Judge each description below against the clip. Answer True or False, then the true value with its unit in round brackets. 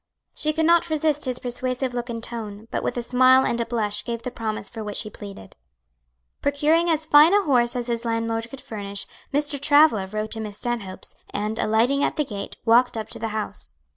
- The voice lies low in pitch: False (235 Hz)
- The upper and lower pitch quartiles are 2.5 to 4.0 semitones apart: False (4.4 semitones)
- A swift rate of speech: True (210 wpm)